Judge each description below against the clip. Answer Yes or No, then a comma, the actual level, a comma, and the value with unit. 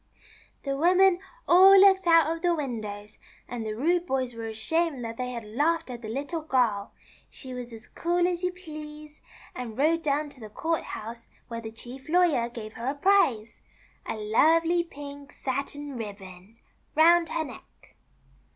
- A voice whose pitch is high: Yes, very high, 280 Hz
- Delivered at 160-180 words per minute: Yes, average, 175 wpm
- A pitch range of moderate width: No, wide, 6.3 semitones